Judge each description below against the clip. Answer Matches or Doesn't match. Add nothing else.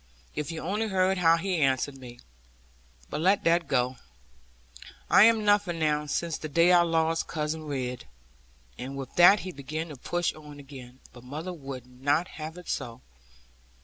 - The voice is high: Doesn't match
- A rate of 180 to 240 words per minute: Doesn't match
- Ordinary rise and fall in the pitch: Matches